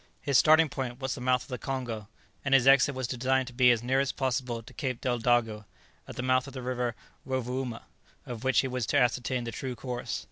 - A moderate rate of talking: No, fast, 225 wpm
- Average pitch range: No, narrow, 1.5 semitones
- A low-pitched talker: Yes, low, 125 Hz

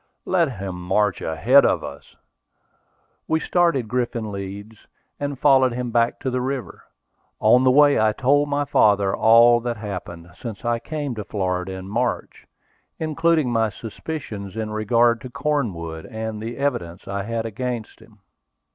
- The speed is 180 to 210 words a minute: No, average, 155 wpm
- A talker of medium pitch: No, low, 115 Hz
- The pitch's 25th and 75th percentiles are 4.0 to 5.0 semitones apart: Yes, average, 4.4 semitones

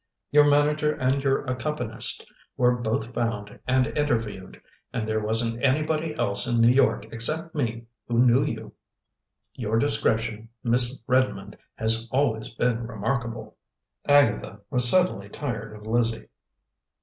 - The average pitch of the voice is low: Yes, low, 120 Hz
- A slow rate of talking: Yes, slow, 130 wpm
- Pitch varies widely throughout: No, average, 3.6 semitones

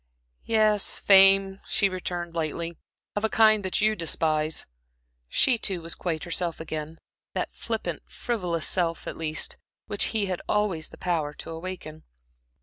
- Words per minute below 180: Yes, average, 145 wpm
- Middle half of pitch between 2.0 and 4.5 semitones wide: Yes, average, 3.6 semitones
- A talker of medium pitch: Yes, medium, 180 Hz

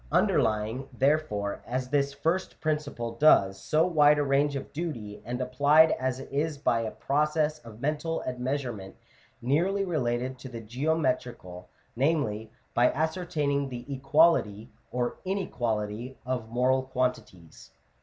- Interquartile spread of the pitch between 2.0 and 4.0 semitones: No, average, 4.4 semitones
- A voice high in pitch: No, low, 130 Hz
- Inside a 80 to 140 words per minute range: Yes, slow, 135 wpm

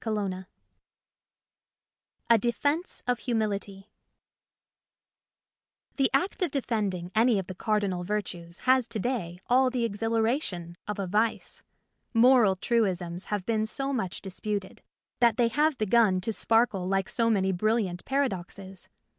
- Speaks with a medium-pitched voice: No, high, 215 Hz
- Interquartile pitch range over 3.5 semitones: Yes, average, 4.0 semitones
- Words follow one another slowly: Yes, slow, 130 wpm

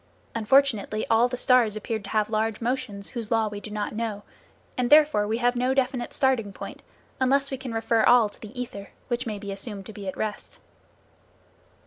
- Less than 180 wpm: No, average, 195 wpm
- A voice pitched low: No, high, 225 Hz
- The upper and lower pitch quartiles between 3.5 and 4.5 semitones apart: No, average, 3.1 semitones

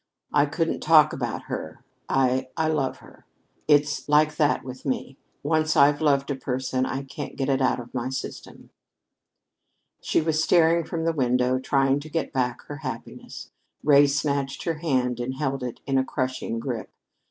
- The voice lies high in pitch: No, medium, 140 Hz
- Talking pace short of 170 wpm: No, average, 175 wpm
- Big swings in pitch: No, average, 2.8 semitones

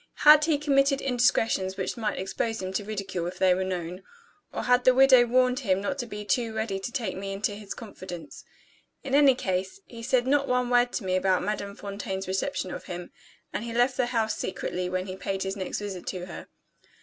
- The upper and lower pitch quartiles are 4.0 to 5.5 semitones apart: Yes, average, 4.8 semitones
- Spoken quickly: Yes, fast, 215 wpm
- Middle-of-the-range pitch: No, high, 210 Hz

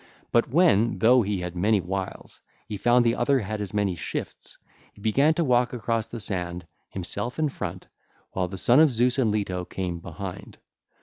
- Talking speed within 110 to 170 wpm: No, average, 185 wpm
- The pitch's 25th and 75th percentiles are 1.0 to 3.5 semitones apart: No, average, 4.5 semitones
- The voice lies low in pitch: Yes, low, 110 Hz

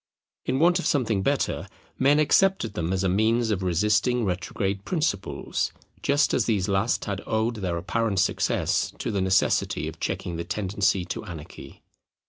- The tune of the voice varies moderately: Yes, average, 4.1 semitones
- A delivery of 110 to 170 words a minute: Yes, average, 160 wpm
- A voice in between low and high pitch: No, low, 100 Hz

